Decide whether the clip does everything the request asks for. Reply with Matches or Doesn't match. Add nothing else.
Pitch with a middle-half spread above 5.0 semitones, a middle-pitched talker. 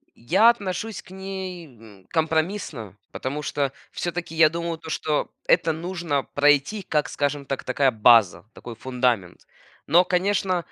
Matches